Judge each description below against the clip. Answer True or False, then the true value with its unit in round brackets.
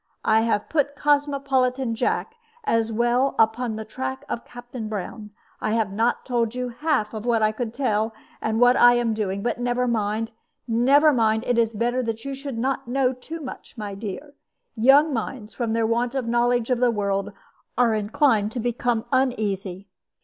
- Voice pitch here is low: False (235 Hz)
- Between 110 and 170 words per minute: False (180 wpm)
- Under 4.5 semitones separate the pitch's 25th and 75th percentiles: True (2.5 semitones)